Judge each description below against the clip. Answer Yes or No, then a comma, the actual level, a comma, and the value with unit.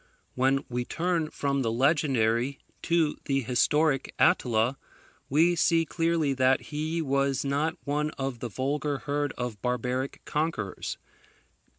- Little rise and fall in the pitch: No, average, 3.2 semitones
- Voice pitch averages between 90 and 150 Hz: Yes, medium, 140 Hz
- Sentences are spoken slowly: Yes, slow, 125 wpm